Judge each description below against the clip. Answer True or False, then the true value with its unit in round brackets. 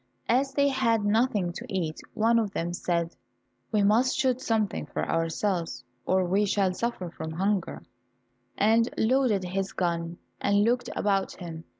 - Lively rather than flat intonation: False (4.6 semitones)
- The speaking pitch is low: False (200 Hz)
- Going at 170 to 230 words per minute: False (155 wpm)